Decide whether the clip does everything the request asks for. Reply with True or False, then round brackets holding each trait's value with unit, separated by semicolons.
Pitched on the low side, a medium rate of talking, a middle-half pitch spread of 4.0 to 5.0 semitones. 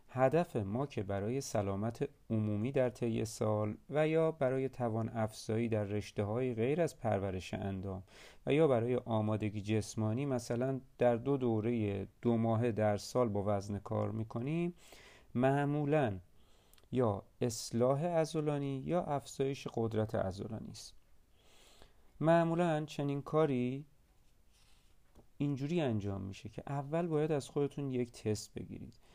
True (120 Hz; 125 wpm; 4.6 semitones)